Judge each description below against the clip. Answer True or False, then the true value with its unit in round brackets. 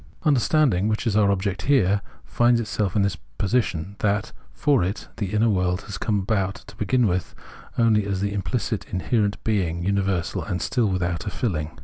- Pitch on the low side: True (100 Hz)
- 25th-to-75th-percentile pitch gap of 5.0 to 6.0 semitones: False (3.1 semitones)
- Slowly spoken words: False (175 wpm)